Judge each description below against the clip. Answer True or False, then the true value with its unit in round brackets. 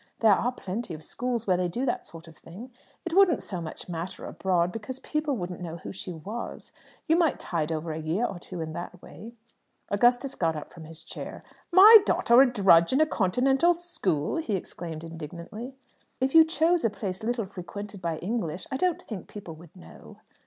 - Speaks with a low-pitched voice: False (200 Hz)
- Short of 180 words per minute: False (200 wpm)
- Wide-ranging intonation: True (7.1 semitones)